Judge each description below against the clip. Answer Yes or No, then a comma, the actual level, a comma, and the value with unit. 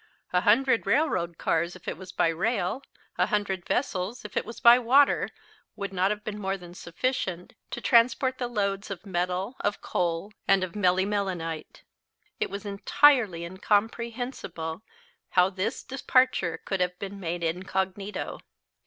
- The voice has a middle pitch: No, high, 195 Hz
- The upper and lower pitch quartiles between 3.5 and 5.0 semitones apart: Yes, average, 4.0 semitones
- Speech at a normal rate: Yes, average, 150 wpm